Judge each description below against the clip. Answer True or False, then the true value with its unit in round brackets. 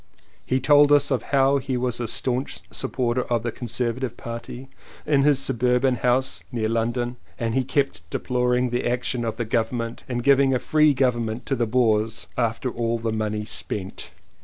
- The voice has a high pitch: False (125 Hz)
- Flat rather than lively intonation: True (2.2 semitones)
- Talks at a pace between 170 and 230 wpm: True (180 wpm)